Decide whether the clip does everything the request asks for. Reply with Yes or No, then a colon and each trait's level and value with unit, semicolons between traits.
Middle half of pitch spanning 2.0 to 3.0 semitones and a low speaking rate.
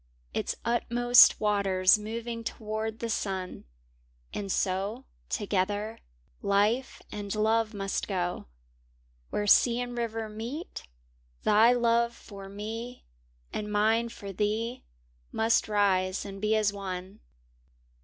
Yes: narrow, 2.5 semitones; slow, 115 wpm